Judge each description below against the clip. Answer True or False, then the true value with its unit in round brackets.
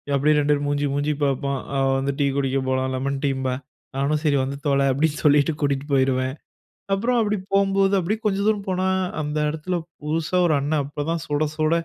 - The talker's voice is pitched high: False (145 Hz)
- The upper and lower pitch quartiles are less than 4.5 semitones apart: True (3.4 semitones)